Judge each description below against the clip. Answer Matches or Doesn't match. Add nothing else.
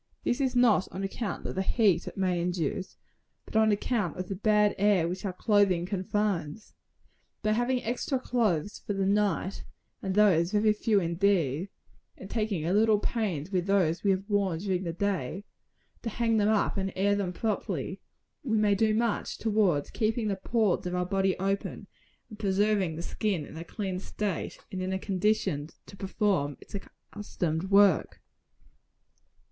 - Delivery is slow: Doesn't match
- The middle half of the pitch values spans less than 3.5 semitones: Matches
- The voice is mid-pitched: Doesn't match